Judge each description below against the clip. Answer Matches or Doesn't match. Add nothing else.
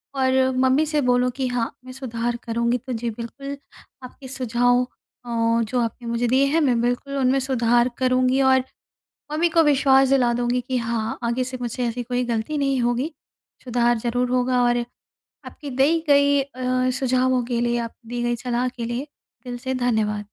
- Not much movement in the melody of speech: Matches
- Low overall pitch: Doesn't match